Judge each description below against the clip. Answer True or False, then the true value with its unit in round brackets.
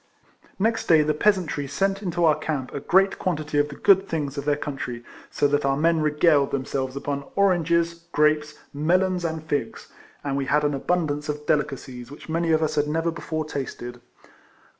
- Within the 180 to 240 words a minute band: True (185 wpm)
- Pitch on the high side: False (150 Hz)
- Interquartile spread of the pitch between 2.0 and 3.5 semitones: True (3.0 semitones)